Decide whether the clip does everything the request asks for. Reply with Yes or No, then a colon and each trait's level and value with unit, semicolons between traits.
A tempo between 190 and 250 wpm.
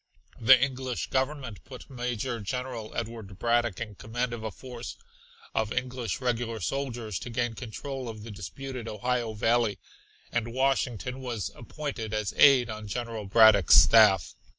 No: average, 145 wpm